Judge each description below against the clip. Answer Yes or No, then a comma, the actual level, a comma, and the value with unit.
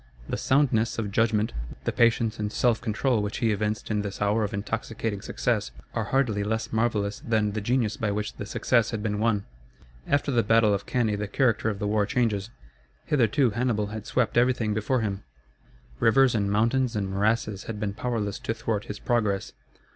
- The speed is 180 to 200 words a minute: Yes, average, 185 wpm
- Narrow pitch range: Yes, narrow, 2.2 semitones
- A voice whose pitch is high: No, low, 110 Hz